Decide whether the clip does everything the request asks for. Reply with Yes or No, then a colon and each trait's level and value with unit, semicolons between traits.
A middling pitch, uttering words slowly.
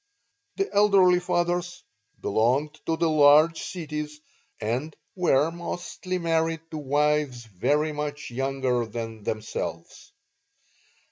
Yes: medium, 150 Hz; slow, 105 wpm